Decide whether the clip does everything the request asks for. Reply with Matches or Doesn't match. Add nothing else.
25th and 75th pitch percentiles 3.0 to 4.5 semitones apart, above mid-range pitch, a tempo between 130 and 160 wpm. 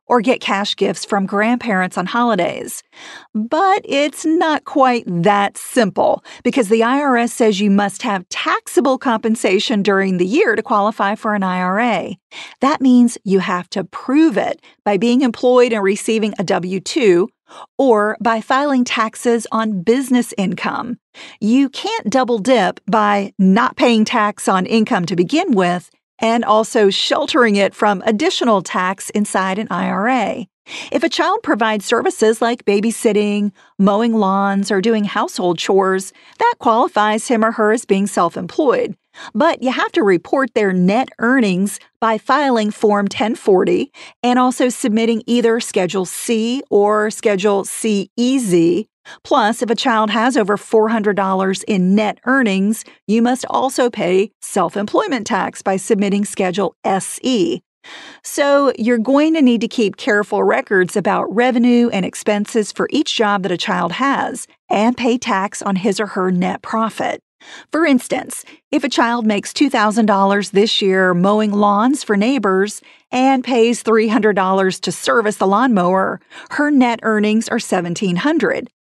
Matches